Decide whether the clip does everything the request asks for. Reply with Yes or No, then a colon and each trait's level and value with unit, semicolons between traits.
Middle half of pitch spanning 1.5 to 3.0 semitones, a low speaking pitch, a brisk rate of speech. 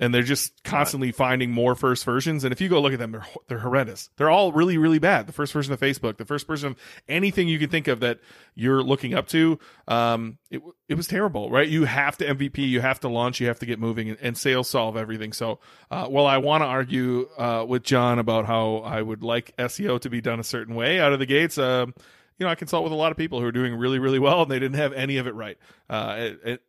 No: average, 3.6 semitones; low, 130 Hz; fast, 270 wpm